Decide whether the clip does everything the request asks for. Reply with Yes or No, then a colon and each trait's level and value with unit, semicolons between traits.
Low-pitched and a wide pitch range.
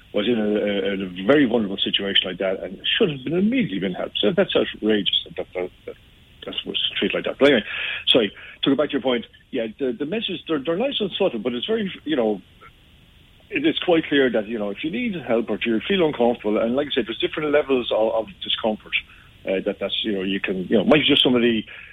Yes: low, 120 Hz; wide, 6.8 semitones